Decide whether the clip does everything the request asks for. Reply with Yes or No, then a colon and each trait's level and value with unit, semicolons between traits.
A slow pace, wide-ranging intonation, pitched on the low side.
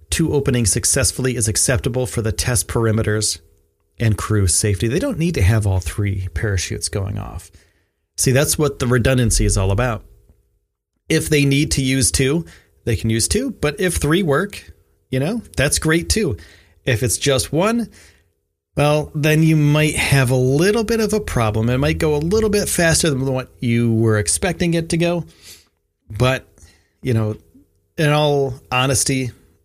No: average, 170 wpm; wide, 7.3 semitones; low, 115 Hz